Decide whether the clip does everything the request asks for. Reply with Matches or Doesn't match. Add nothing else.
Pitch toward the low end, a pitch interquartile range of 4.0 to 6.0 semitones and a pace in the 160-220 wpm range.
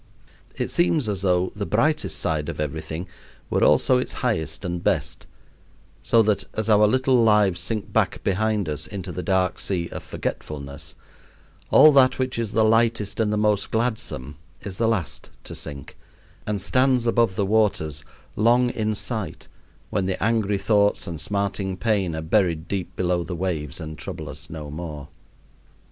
Matches